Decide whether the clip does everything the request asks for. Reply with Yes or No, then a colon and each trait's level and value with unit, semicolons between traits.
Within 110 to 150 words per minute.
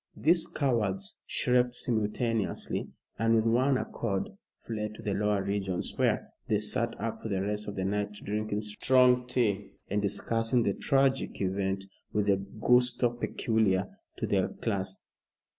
Yes: average, 145 wpm